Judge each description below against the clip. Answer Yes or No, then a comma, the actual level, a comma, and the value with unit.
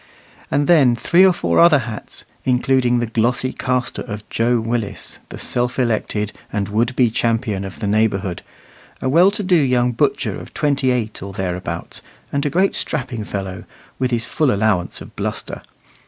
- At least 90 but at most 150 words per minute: No, average, 170 wpm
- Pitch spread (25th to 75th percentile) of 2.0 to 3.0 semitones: No, average, 3.7 semitones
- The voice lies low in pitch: Yes, low, 120 Hz